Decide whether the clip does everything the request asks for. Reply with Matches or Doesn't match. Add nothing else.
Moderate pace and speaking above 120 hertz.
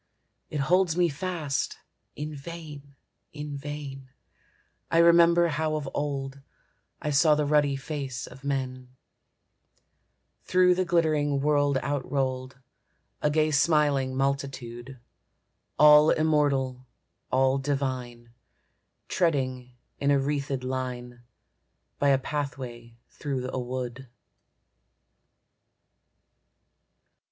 Doesn't match